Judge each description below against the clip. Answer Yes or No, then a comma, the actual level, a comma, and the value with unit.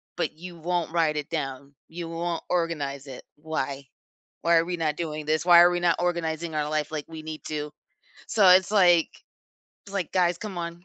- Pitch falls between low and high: Yes, medium, 165 Hz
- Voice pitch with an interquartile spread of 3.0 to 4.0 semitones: No, narrow, 2.4 semitones